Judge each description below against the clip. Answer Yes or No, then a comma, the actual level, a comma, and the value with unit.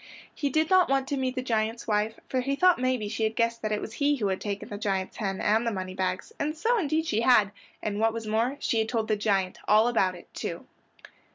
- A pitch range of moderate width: Yes, average, 4.0 semitones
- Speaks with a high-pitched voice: Yes, high, 225 Hz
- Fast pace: Yes, fast, 250 wpm